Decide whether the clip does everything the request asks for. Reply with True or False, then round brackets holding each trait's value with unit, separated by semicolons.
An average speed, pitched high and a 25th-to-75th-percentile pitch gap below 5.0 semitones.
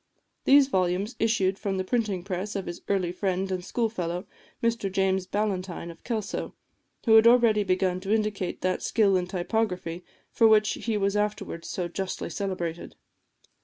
True (165 wpm; 195 Hz; 2.8 semitones)